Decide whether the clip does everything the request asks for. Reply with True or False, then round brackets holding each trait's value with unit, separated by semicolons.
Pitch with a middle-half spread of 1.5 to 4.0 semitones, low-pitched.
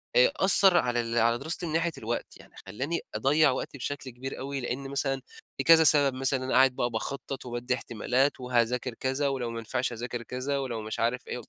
True (2.5 semitones; 130 Hz)